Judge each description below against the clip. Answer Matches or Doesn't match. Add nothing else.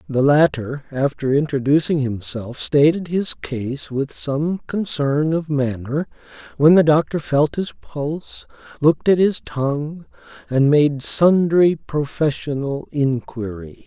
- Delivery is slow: Matches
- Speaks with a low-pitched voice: Doesn't match